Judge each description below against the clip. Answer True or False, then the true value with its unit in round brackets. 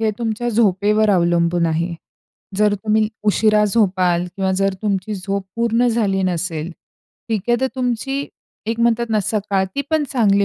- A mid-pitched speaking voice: False (210 Hz)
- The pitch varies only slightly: False (3.3 semitones)